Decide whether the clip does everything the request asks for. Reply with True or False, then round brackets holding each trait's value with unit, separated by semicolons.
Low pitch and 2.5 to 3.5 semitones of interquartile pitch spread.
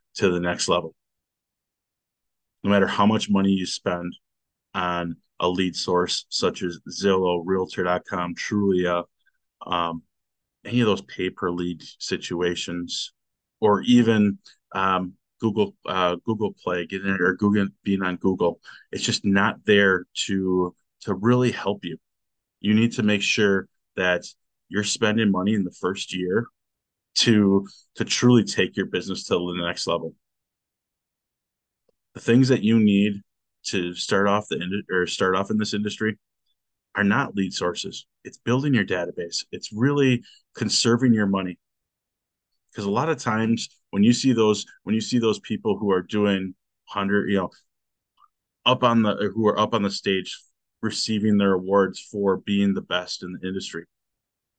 True (100 Hz; 2.9 semitones)